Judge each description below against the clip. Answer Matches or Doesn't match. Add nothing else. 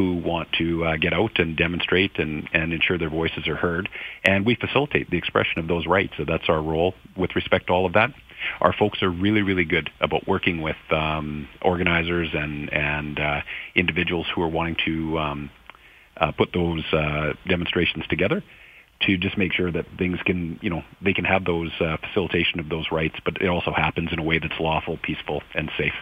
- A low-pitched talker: Matches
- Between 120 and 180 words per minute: Doesn't match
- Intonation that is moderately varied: Doesn't match